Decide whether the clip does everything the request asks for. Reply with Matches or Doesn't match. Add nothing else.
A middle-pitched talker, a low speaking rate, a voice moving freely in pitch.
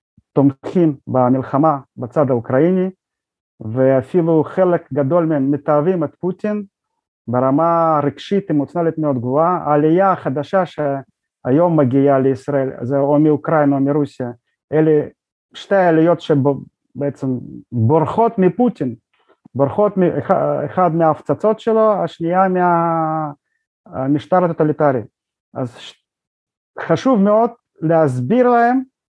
Doesn't match